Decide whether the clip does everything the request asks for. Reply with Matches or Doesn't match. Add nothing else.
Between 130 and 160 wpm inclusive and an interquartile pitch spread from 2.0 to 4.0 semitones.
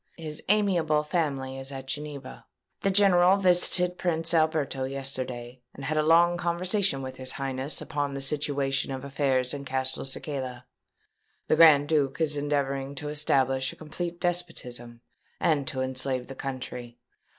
Matches